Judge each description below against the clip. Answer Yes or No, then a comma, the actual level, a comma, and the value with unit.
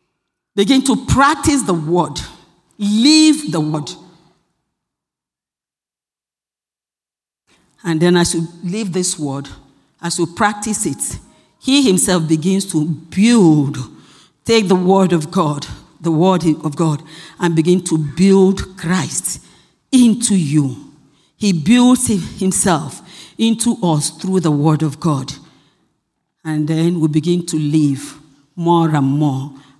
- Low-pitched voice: No, medium, 170 Hz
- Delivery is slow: Yes, slow, 120 wpm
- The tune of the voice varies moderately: Yes, average, 3.8 semitones